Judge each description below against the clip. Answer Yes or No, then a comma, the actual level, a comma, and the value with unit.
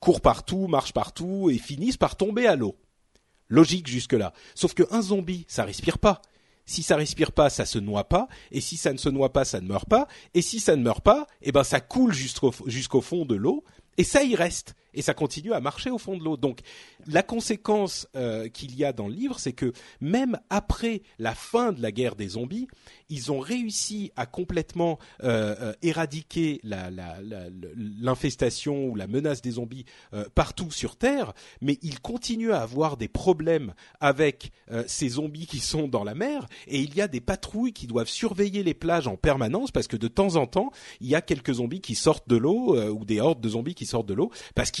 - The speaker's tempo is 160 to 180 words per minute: No, fast, 220 wpm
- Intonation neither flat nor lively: No, wide, 7.8 semitones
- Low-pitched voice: No, medium, 150 Hz